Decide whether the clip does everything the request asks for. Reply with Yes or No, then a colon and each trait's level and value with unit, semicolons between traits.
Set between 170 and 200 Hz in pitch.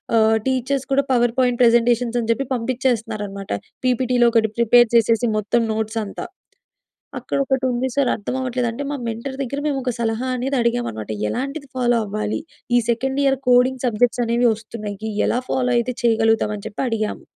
No: high, 240 Hz